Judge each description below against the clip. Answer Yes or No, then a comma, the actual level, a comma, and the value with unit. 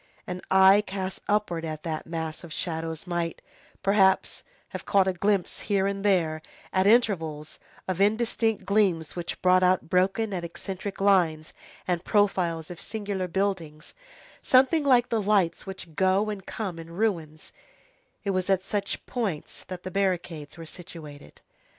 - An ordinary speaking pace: Yes, average, 150 wpm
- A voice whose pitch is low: No, medium, 185 Hz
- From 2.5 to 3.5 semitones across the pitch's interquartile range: Yes, average, 3.2 semitones